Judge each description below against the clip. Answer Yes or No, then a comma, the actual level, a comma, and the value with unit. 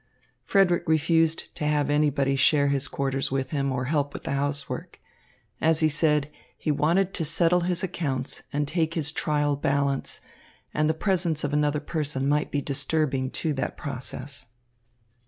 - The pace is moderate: Yes, average, 160 wpm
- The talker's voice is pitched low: No, medium, 145 Hz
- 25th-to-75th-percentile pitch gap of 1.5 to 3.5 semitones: Yes, narrow, 2.4 semitones